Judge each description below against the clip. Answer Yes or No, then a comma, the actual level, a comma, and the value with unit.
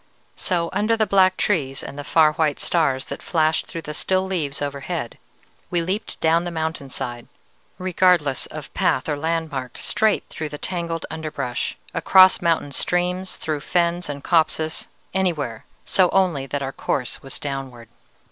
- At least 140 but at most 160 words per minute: Yes, average, 155 wpm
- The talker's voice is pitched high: No, medium, 160 Hz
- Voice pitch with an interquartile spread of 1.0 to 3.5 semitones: No, average, 4.1 semitones